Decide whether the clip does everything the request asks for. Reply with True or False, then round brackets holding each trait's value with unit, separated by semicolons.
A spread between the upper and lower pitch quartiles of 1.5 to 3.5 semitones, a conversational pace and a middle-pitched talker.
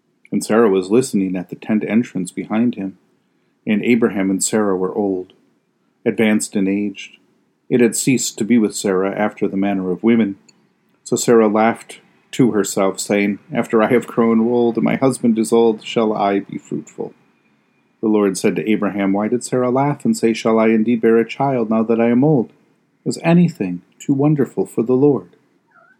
False (2.9 semitones; 185 wpm; 110 Hz)